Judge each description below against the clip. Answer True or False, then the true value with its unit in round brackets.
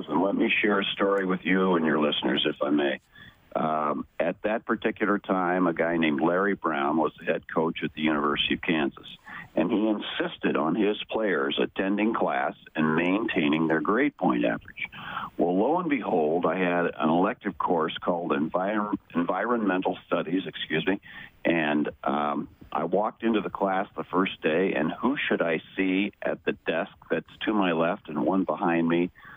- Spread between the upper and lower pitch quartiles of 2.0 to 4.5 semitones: True (3.6 semitones)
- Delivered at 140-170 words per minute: False (180 wpm)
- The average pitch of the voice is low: True (90 Hz)